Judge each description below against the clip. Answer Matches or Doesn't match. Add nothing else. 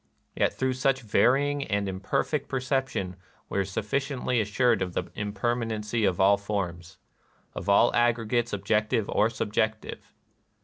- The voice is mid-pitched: Doesn't match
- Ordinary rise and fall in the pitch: Matches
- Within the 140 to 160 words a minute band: Matches